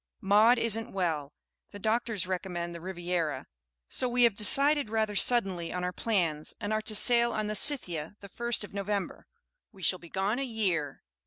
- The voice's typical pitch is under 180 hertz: No, high, 200 Hz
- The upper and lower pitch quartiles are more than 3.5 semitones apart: Yes, average, 4.1 semitones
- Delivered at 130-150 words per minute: No, average, 180 wpm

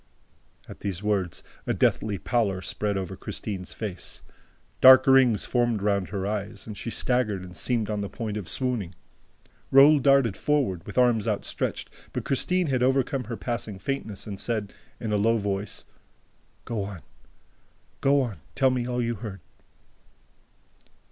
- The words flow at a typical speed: Yes, average, 155 wpm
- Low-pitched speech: Yes, low, 110 Hz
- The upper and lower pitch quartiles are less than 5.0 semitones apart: Yes, average, 4.0 semitones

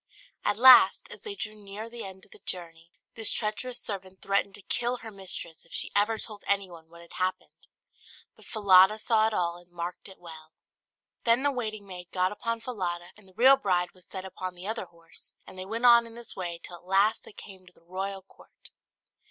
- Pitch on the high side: Yes, high, 195 Hz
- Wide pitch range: No, average, 3.6 semitones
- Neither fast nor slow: No, fast, 215 wpm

